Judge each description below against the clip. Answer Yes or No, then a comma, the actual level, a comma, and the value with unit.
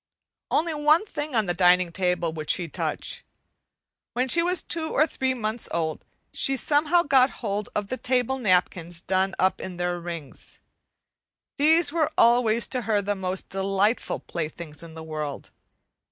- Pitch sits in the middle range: No, high, 205 Hz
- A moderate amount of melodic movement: No, wide, 7.2 semitones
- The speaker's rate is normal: Yes, average, 160 wpm